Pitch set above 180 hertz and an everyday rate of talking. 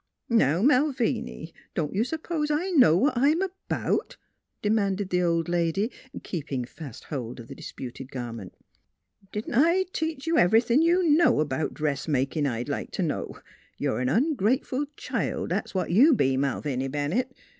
Yes: high, 190 Hz; average, 160 wpm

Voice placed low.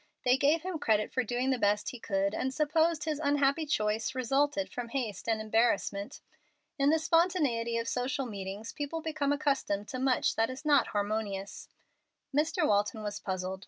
No: very high, 255 Hz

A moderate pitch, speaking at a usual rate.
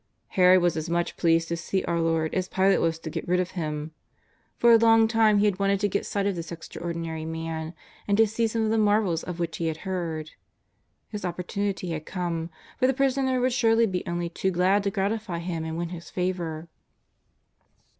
No: medium, 180 Hz; fast, 215 wpm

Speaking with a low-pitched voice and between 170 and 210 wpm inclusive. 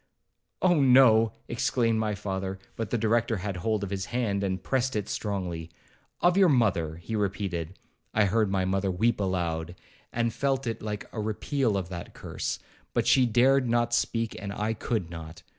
Yes: low, 105 Hz; average, 175 wpm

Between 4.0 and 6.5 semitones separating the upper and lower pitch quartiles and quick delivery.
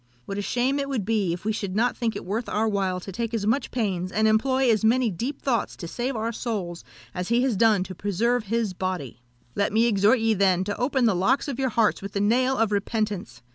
No: average, 3.6 semitones; fast, 245 wpm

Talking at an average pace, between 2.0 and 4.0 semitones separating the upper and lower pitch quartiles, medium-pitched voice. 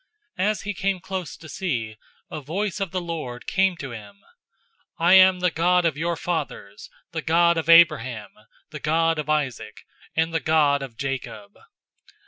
No: average, 170 wpm; average, 4.6 semitones; medium, 165 Hz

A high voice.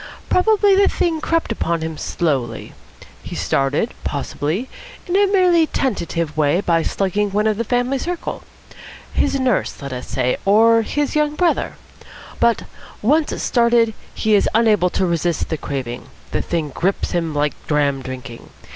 Yes: high, 205 Hz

